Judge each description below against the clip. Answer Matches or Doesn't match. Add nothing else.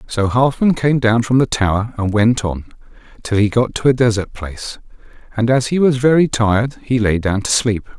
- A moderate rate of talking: Doesn't match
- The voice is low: Matches